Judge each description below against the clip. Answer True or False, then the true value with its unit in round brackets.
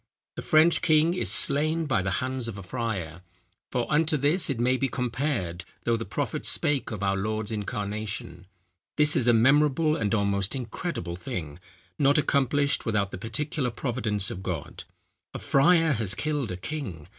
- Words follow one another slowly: False (170 wpm)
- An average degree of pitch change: False (6.6 semitones)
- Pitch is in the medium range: False (120 Hz)